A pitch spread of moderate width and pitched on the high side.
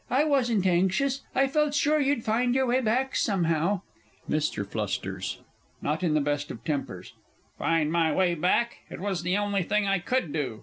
No: wide, 7.6 semitones; high, 195 Hz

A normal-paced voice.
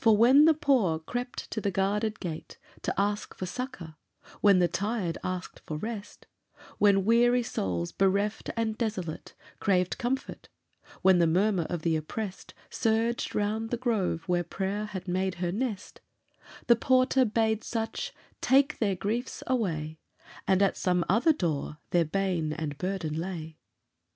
Yes: average, 150 wpm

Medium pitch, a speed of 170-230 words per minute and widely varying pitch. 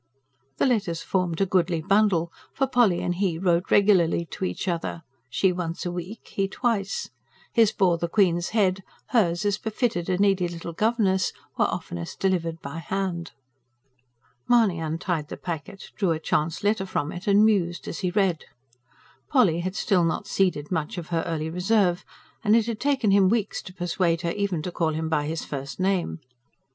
No: medium, 180 Hz; average, 180 wpm; average, 3.2 semitones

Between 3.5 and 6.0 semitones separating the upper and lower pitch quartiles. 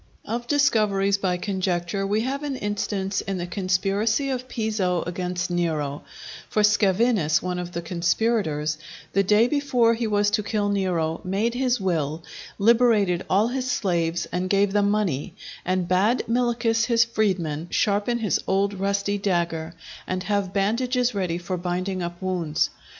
Yes: average, 3.9 semitones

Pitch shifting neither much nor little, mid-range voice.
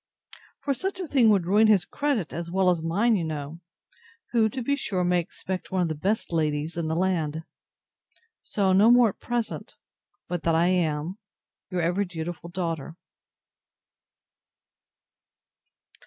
Yes: average, 4.7 semitones; medium, 180 Hz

